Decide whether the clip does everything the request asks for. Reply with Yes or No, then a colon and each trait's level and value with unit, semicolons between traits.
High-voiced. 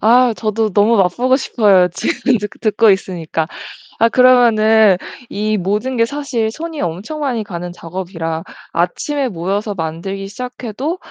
Yes: high, 215 Hz